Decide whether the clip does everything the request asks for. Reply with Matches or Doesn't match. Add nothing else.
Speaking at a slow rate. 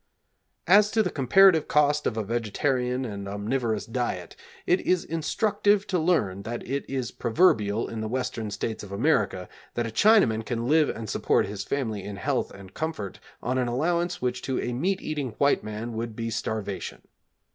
Doesn't match